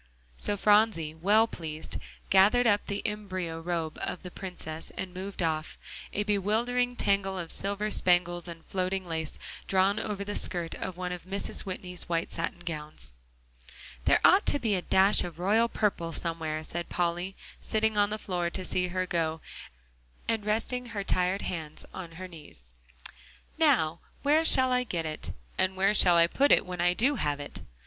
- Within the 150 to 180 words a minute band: Yes, average, 175 wpm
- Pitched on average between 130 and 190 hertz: Yes, medium, 185 Hz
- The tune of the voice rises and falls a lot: No, average, 3.7 semitones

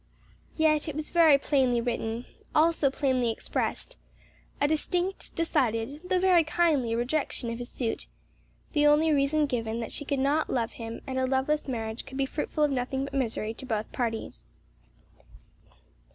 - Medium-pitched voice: No, very high, 270 Hz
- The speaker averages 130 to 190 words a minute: Yes, average, 160 wpm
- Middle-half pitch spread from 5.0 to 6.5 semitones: No, average, 4.3 semitones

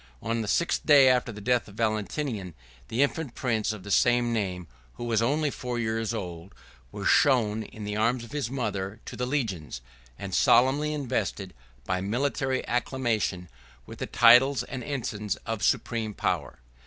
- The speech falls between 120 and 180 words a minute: Yes, average, 165 wpm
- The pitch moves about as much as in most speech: Yes, average, 3.7 semitones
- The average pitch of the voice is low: Yes, low, 115 Hz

